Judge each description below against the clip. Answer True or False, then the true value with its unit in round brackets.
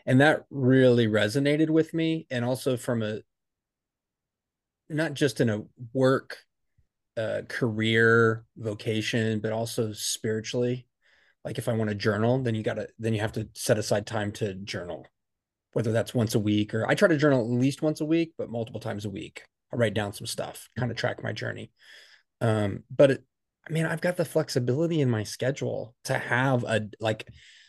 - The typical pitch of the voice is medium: False (120 Hz)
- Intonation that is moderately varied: True (3.5 semitones)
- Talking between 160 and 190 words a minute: True (185 wpm)